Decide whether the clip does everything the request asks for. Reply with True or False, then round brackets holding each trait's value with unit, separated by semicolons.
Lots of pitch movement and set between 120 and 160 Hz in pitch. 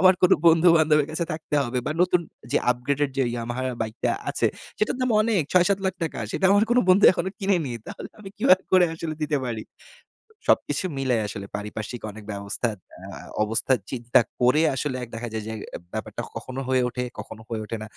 True (7.0 semitones; 140 Hz)